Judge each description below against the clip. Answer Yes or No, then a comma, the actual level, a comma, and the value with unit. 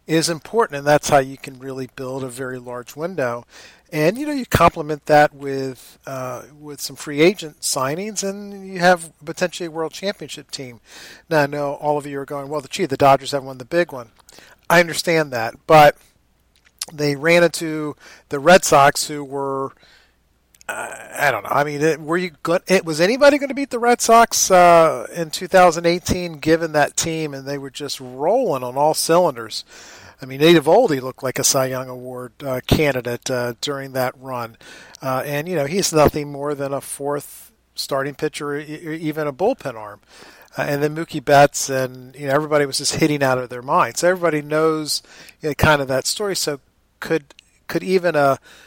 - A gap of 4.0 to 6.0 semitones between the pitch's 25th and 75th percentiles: No, average, 3.6 semitones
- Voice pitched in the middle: Yes, medium, 145 Hz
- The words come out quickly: No, average, 195 wpm